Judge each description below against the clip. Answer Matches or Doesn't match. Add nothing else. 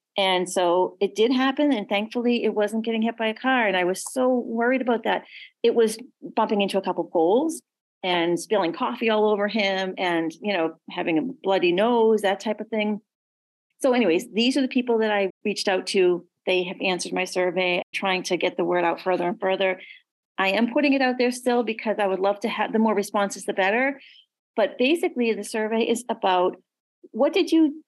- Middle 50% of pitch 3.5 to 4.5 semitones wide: Matches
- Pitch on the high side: Matches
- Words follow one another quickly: Matches